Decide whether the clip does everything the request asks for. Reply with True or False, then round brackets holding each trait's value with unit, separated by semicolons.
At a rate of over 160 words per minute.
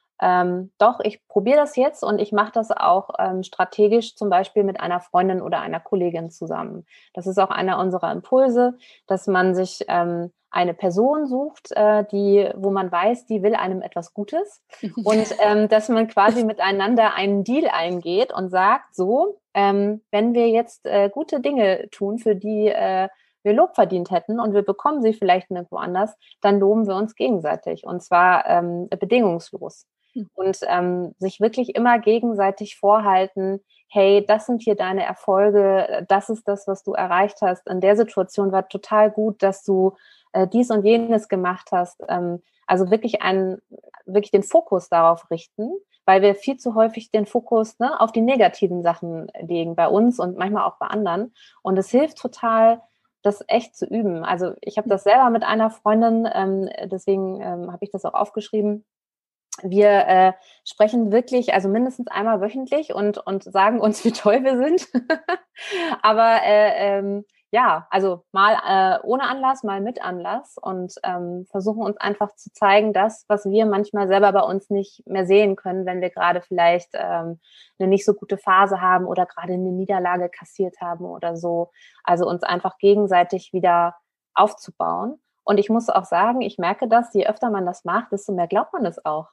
True (180 wpm)